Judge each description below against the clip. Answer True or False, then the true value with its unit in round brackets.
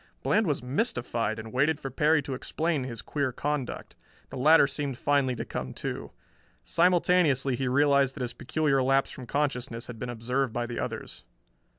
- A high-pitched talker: False (135 Hz)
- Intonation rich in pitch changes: False (3.0 semitones)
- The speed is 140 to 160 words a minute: False (175 wpm)